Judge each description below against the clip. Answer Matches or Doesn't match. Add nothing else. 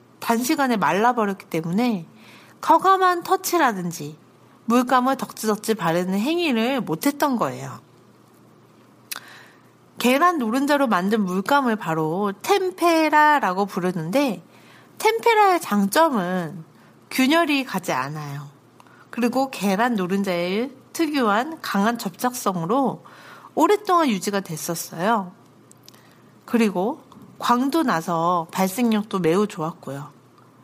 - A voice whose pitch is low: Doesn't match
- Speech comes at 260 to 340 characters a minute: Doesn't match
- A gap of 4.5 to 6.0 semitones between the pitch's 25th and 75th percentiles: Doesn't match